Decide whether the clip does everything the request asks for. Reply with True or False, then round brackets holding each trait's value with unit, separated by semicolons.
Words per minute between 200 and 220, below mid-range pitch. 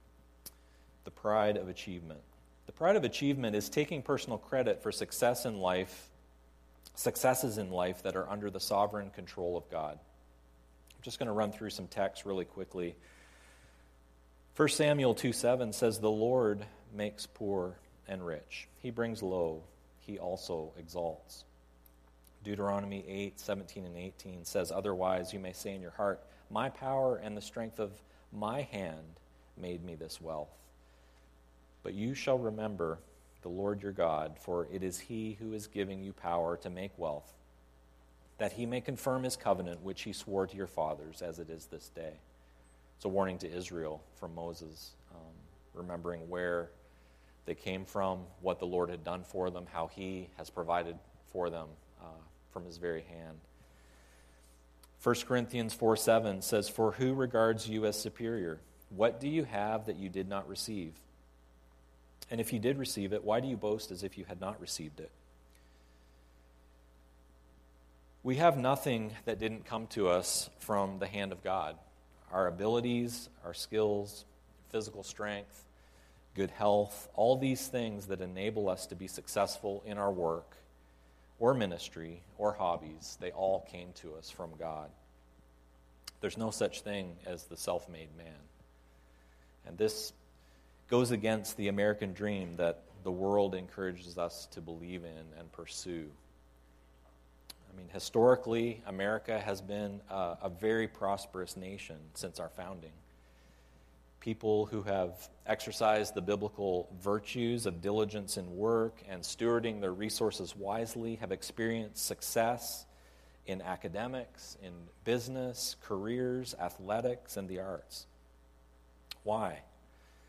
False (145 wpm; 90 Hz)